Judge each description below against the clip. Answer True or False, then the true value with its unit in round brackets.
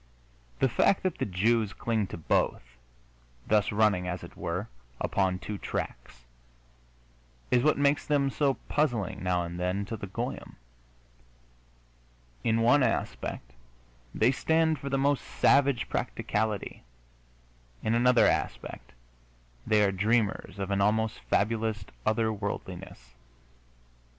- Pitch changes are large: False (4.5 semitones)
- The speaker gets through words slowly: True (125 wpm)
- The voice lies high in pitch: False (110 Hz)